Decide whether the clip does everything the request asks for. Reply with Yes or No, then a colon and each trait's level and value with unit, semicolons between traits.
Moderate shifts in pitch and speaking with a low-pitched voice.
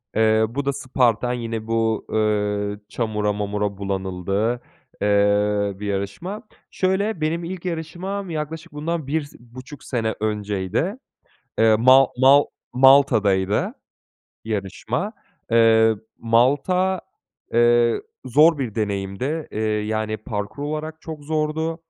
No: wide, 6.5 semitones; low, 115 Hz